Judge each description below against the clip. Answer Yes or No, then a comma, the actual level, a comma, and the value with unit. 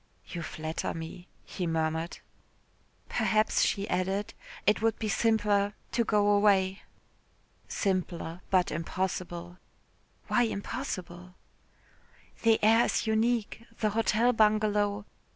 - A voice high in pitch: Yes, high, 200 Hz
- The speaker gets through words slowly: Yes, slow, 105 wpm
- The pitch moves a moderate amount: Yes, average, 3.4 semitones